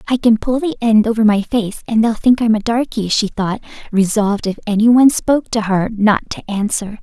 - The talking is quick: Yes, fast, 215 wpm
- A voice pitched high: Yes, high, 220 Hz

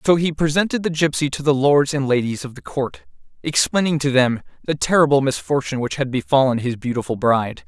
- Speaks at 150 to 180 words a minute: No, average, 195 wpm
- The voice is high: No, medium, 140 Hz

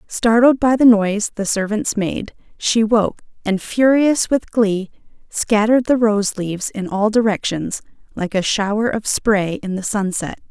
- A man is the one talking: No, female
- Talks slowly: No, average, 160 wpm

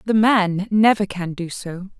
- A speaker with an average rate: Yes, average, 180 wpm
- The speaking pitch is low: No, high, 195 Hz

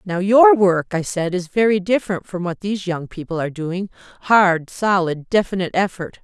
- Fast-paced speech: No, average, 175 wpm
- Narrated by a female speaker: Yes, female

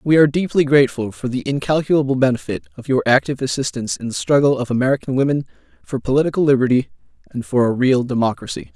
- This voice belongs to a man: Yes, male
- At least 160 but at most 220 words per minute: Yes, average, 180 wpm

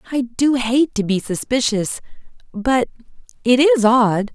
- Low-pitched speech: No, high, 235 Hz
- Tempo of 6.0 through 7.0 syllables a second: No, 4.0 syllables/s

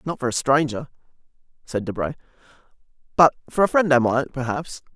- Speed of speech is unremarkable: Yes, average, 155 wpm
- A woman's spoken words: No, male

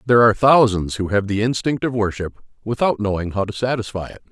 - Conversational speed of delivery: No, fast, 210 wpm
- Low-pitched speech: Yes, low, 110 Hz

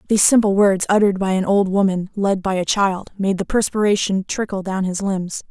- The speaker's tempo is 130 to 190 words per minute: No, fast, 205 wpm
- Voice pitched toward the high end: Yes, high, 195 Hz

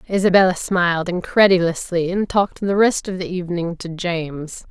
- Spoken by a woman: Yes, female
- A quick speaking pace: No, average, 155 wpm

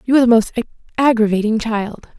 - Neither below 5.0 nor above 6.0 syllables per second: No, 6.2 syllables/s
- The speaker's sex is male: No, female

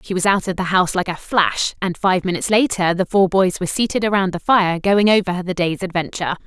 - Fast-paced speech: Yes, fast, 240 wpm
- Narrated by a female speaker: Yes, female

